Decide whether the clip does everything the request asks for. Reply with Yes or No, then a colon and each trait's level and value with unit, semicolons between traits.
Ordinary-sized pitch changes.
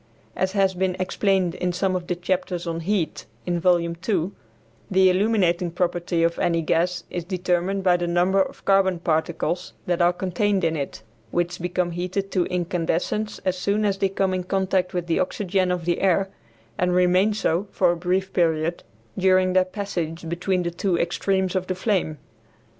No: narrow, 1.7 semitones